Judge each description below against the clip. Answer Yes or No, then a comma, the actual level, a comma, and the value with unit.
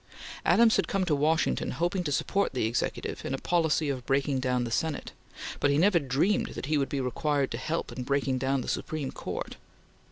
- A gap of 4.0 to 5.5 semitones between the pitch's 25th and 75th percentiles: No, average, 3.6 semitones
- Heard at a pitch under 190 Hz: Yes, medium, 140 Hz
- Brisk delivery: Yes, fast, 210 wpm